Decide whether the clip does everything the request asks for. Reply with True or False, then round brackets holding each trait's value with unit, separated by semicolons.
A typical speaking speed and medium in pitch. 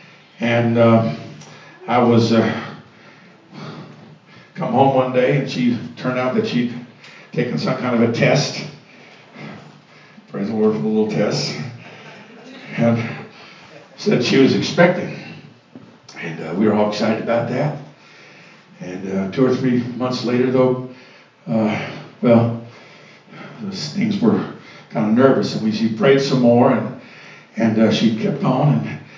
False (145 wpm; 125 Hz)